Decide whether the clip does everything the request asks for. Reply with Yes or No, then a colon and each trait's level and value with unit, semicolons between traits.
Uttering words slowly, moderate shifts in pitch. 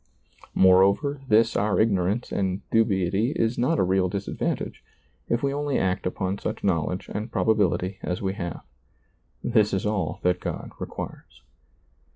No: average, 145 wpm; average, 3.4 semitones